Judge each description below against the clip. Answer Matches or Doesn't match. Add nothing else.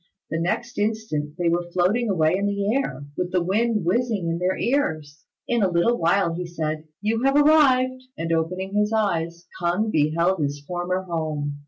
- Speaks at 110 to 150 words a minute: Doesn't match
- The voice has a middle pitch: Matches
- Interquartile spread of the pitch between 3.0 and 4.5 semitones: Doesn't match